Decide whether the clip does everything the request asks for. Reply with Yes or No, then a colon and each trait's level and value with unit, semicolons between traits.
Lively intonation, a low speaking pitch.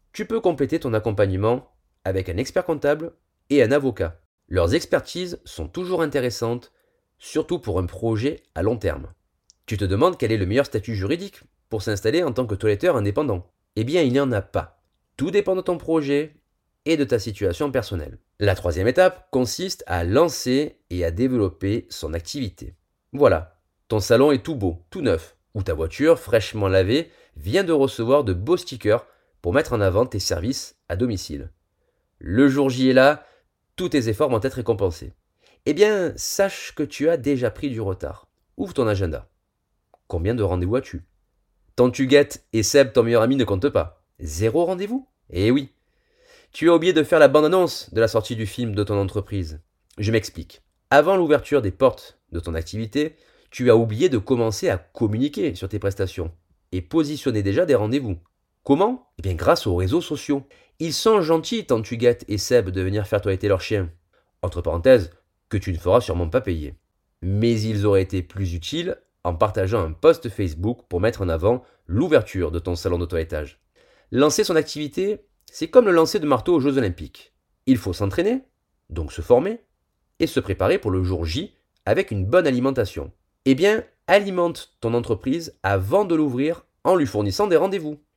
Yes: wide, 7.9 semitones; low, 115 Hz